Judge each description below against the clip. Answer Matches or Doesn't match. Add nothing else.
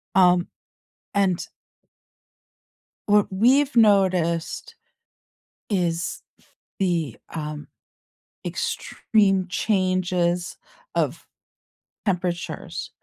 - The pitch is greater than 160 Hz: Matches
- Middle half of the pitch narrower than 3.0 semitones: Matches